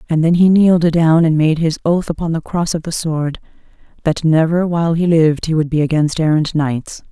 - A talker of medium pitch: Yes, medium, 160 Hz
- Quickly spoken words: Yes, fast, 220 wpm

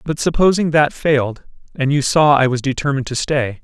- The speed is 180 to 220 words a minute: Yes, average, 200 wpm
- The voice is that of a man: Yes, male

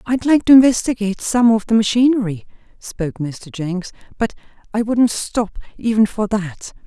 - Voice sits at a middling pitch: No, high, 220 Hz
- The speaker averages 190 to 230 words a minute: No, average, 155 wpm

